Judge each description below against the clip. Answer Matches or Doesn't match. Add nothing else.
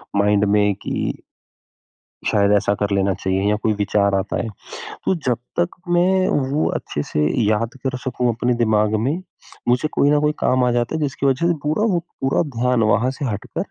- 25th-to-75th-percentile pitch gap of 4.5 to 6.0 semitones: Matches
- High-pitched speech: Doesn't match